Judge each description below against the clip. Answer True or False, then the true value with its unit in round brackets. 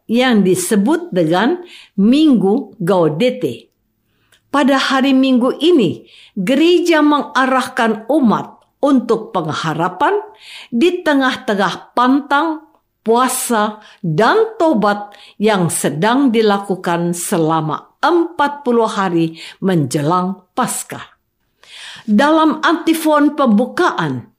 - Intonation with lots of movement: True (6.9 semitones)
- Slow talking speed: True (75 wpm)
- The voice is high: True (240 Hz)